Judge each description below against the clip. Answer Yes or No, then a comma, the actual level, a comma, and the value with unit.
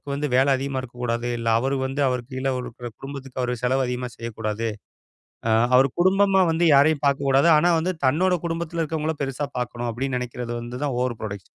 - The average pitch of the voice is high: No, low, 130 Hz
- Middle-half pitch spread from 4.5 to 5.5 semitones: No, average, 3.4 semitones